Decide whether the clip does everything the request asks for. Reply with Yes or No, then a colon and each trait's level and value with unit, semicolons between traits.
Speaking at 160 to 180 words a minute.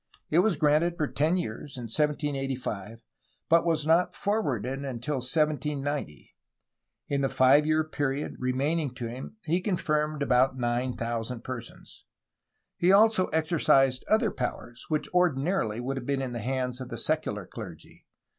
No: average, 145 wpm